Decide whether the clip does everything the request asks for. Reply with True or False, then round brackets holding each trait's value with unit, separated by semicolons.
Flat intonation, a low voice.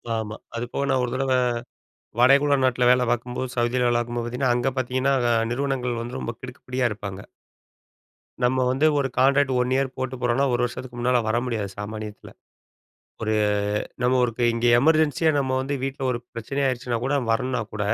True (1.9 semitones; 125 Hz)